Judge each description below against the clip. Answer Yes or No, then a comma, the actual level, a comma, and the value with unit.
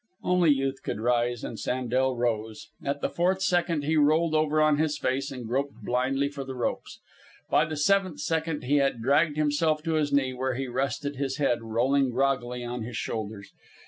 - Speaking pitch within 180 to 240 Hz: No, low, 135 Hz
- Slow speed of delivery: No, average, 190 wpm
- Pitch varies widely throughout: No, average, 3.7 semitones